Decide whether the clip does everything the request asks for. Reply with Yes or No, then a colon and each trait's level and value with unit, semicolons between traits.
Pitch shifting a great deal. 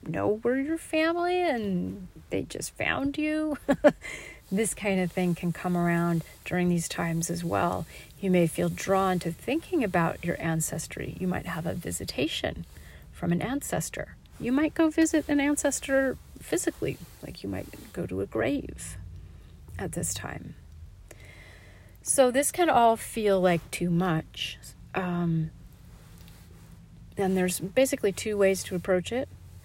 Yes: wide, 8.9 semitones